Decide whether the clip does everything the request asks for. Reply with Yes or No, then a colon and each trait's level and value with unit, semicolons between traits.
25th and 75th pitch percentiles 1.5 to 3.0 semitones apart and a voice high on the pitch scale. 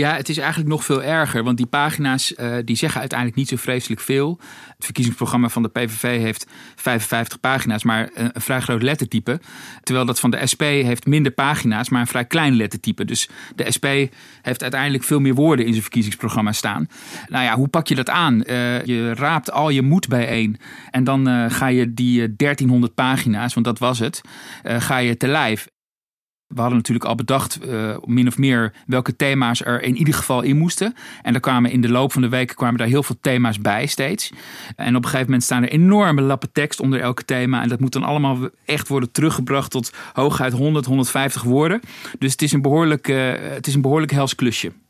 No: narrow, 2.5 semitones; low, 130 Hz